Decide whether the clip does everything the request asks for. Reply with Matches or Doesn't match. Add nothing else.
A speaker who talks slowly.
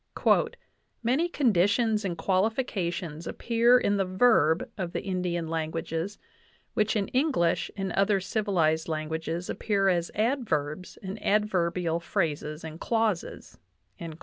Matches